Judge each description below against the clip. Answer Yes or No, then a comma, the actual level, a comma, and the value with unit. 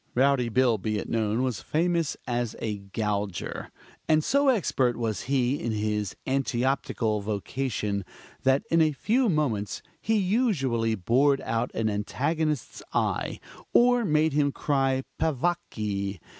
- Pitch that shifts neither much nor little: No, wide, 5.9 semitones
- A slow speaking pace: Yes, slow, 130 wpm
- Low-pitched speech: Yes, low, 130 Hz